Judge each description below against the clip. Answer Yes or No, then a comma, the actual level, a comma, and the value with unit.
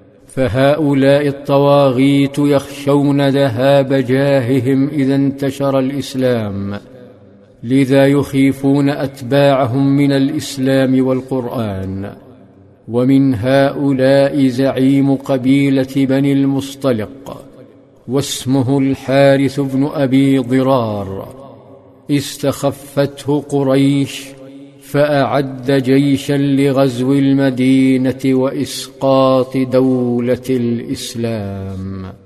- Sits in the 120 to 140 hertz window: Yes, low, 135 Hz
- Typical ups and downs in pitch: No, narrow, 1.1 semitones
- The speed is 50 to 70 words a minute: Yes, slow, 65 wpm